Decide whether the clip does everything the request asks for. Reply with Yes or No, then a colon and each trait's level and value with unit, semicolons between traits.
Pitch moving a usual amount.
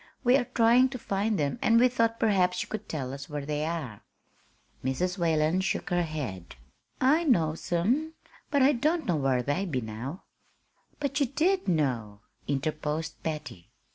No: wide, 8.7 semitones